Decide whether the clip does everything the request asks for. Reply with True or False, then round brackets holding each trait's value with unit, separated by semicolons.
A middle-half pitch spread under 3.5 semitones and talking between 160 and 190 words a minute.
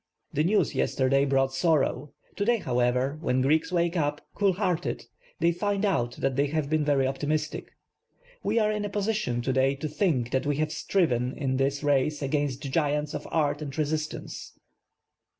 False (3.8 semitones; 175 wpm)